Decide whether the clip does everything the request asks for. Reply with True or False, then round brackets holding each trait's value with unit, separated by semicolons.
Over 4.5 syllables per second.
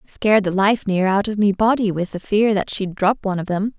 True (5.5 syllables/s)